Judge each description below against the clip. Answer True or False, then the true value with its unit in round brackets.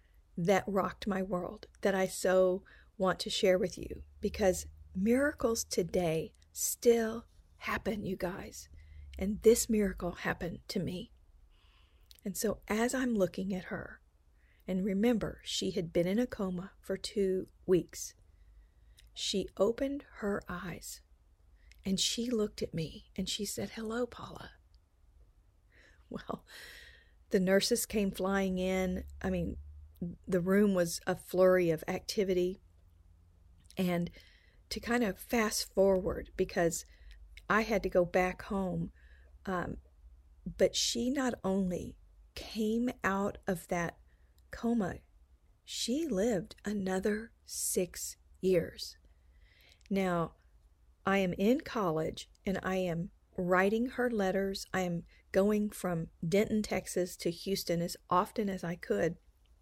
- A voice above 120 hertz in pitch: True (185 Hz)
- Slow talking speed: True (125 wpm)